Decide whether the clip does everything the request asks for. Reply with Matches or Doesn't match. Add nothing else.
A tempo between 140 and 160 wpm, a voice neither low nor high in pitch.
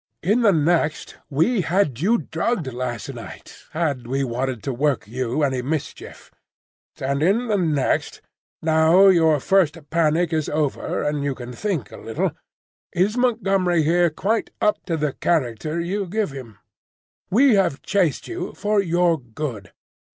Matches